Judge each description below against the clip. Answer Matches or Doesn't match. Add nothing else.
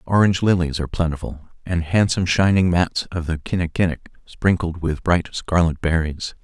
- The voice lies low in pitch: Matches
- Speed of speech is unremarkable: Matches